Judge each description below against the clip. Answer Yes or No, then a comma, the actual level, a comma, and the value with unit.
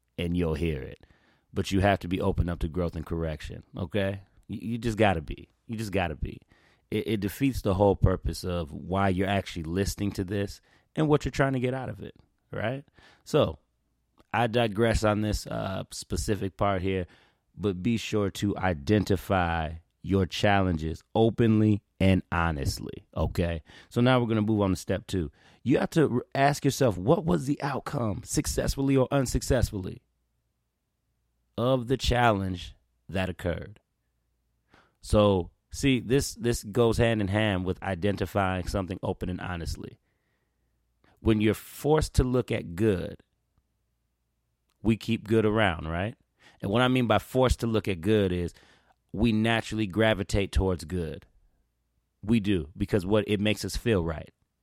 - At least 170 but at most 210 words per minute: No, average, 160 wpm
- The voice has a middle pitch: No, low, 100 Hz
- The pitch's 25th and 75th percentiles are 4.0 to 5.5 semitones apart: Yes, average, 4.3 semitones